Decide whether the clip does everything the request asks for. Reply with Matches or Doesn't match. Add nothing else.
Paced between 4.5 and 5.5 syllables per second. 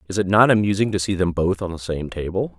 Doesn't match